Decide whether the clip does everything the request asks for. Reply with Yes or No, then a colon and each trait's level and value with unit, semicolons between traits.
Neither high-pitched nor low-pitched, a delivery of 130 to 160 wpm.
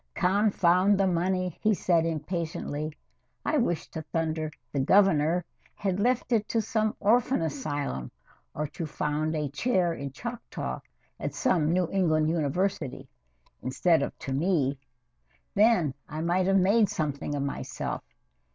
Yes: medium, 170 Hz; average, 140 wpm